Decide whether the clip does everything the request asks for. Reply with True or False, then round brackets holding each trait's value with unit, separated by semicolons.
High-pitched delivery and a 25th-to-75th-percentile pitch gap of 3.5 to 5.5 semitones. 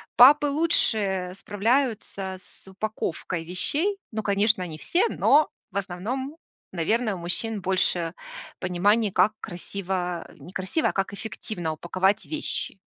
True (200 Hz; 4.1 semitones)